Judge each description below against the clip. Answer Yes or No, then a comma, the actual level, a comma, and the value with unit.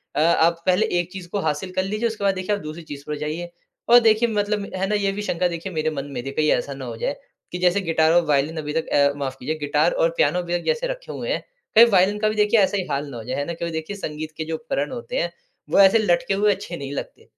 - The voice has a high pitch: No, medium, 175 Hz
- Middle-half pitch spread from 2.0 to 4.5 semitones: No, average, 5.0 semitones